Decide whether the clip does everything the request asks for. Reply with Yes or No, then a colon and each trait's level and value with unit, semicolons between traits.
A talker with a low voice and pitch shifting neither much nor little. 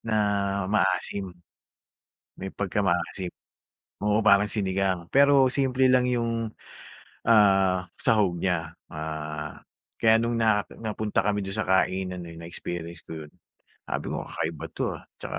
Yes: very low, 95 Hz; average, 4.3 semitones